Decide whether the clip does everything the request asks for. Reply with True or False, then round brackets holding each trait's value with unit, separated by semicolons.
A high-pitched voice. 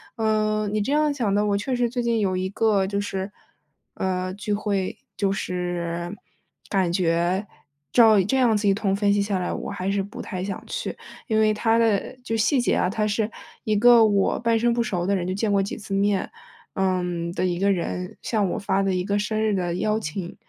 True (200 Hz)